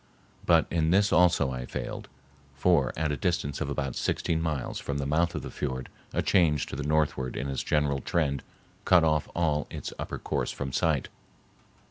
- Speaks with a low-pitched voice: Yes, very low, 75 Hz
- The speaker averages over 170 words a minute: Yes, average, 185 wpm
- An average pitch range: Yes, average, 3.1 semitones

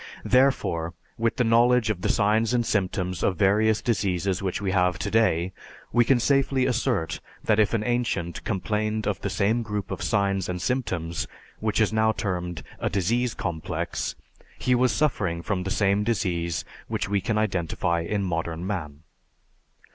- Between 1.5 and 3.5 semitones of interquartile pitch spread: No, average, 4.0 semitones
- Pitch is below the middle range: Yes, low, 100 Hz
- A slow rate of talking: No, average, 160 wpm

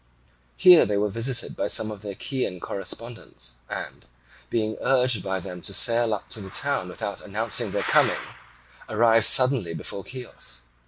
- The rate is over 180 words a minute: No, average, 160 wpm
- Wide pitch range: No, average, 3.7 semitones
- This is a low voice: Yes, low, 110 Hz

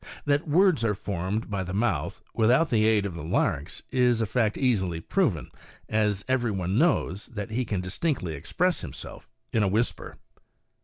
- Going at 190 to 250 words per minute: No, average, 170 wpm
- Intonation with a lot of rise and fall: No, average, 5.0 semitones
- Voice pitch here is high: No, low, 110 Hz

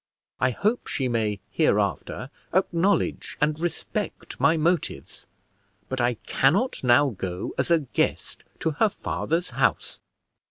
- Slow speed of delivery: Yes, slow, 125 wpm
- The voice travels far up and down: Yes, wide, 6.0 semitones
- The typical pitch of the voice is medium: Yes, medium, 145 Hz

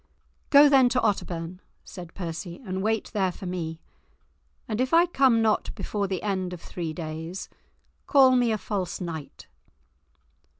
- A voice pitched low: No, high, 190 Hz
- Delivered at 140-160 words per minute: Yes, average, 155 wpm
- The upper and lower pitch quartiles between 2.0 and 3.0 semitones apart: No, average, 4.7 semitones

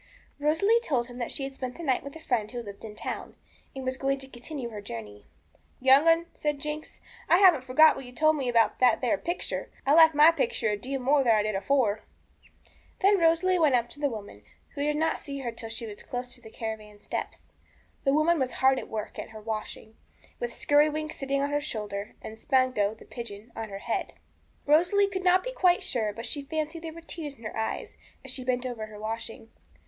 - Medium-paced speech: No, fast, 225 wpm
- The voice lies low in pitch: No, very high, 265 Hz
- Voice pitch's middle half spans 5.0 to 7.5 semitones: Yes, wide, 5.5 semitones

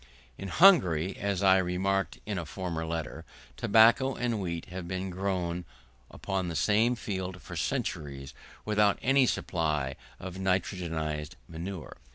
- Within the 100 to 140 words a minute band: Yes, slow, 135 wpm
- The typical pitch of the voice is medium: No, very low, 95 Hz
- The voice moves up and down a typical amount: Yes, average, 3.3 semitones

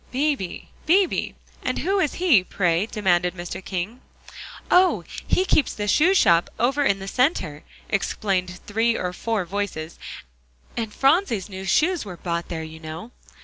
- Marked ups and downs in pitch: Yes, wide, 7.4 semitones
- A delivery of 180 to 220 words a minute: No, average, 150 wpm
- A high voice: Yes, high, 205 Hz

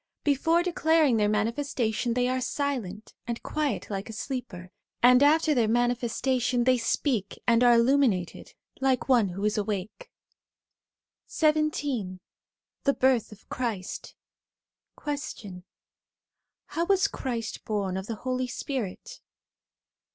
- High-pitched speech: Yes, high, 245 Hz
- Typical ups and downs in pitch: Yes, average, 4.6 semitones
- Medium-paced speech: No, slow, 120 wpm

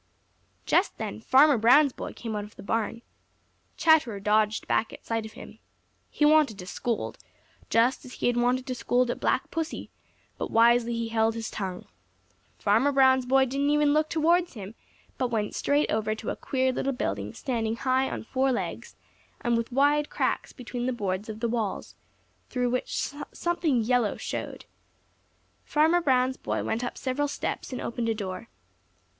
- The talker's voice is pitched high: Yes, high, 245 Hz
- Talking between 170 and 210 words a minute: Yes, average, 175 wpm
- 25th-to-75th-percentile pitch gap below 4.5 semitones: Yes, average, 3.4 semitones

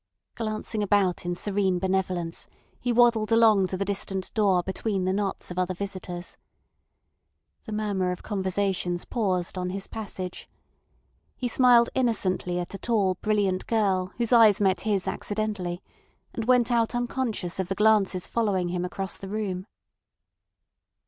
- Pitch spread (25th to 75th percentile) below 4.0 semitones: Yes, average, 2.9 semitones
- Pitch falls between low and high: No, high, 195 Hz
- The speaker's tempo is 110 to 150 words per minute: Yes, average, 145 wpm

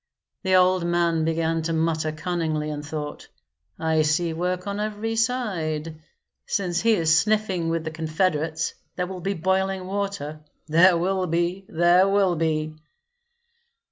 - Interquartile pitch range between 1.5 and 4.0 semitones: Yes, average, 3.0 semitones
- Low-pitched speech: No, medium, 170 Hz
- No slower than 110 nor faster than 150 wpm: Yes, average, 140 wpm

